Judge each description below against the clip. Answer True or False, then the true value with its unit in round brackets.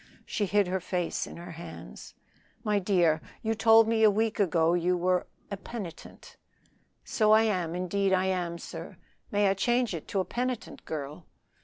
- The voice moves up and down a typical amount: True (3.7 semitones)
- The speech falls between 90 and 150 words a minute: False (175 wpm)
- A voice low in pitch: False (190 Hz)